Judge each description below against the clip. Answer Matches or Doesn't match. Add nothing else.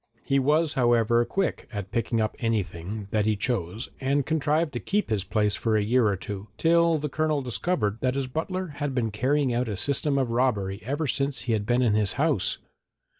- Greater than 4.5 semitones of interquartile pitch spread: Matches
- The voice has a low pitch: Matches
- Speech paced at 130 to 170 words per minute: Doesn't match